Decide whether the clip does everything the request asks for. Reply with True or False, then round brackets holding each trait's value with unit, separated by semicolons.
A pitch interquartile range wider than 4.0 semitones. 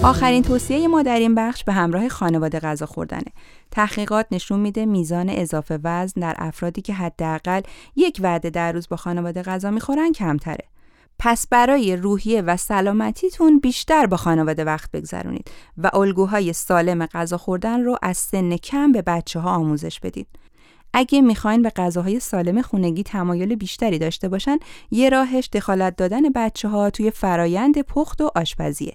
True (5.3 semitones)